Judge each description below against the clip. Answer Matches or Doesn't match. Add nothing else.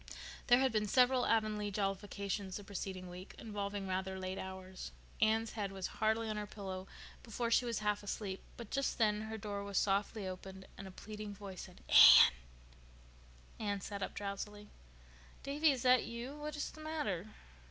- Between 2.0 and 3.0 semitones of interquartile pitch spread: Matches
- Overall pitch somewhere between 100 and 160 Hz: Doesn't match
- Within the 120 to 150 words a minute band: Doesn't match